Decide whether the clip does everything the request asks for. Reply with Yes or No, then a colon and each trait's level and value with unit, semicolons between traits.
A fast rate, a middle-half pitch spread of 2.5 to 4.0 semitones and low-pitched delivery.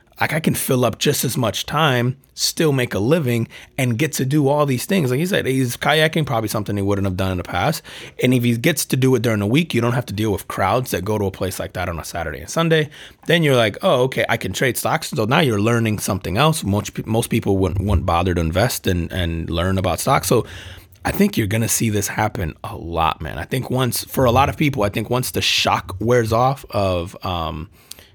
No: fast, 255 wpm; average, 5.3 semitones; low, 115 Hz